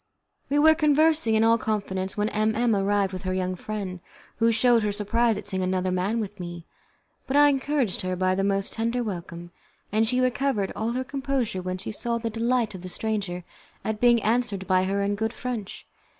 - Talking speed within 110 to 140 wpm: No, fast, 205 wpm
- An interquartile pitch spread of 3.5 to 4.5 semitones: Yes, average, 4.1 semitones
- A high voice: Yes, high, 215 Hz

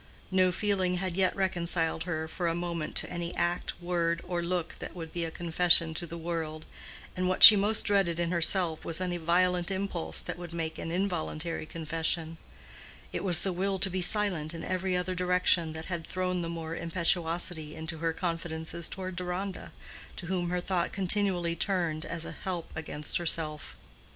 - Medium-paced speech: Yes, average, 180 wpm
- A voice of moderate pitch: Yes, medium, 175 Hz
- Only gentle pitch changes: Yes, narrow, 1.9 semitones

